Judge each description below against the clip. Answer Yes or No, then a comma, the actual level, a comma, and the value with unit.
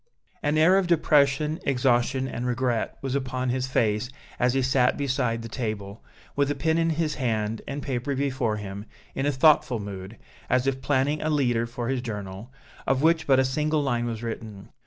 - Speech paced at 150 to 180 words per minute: No, average, 190 wpm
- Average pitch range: Yes, average, 3.5 semitones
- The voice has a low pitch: Yes, low, 130 Hz